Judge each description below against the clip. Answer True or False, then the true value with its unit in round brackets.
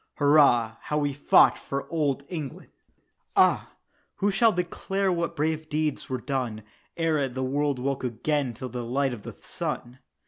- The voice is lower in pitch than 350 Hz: True (140 Hz)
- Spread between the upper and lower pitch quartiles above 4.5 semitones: False (3.4 semitones)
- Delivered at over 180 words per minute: False (160 wpm)